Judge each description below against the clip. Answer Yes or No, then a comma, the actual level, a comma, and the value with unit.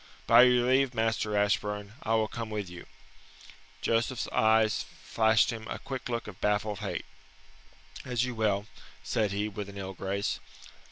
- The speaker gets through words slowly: No, average, 160 wpm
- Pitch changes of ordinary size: No, narrow, 2.1 semitones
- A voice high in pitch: No, low, 110 Hz